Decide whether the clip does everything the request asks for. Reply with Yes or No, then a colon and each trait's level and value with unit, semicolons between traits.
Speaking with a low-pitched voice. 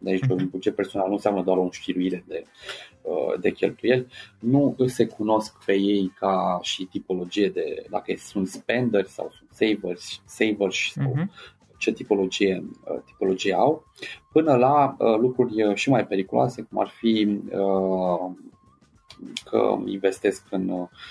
Yes: low, 100 Hz